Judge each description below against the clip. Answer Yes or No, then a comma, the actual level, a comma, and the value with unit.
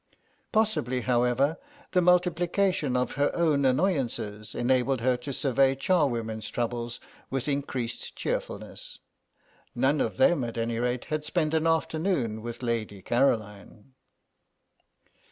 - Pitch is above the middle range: No, low, 130 Hz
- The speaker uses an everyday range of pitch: Yes, average, 4.7 semitones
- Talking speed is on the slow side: Yes, slow, 120 wpm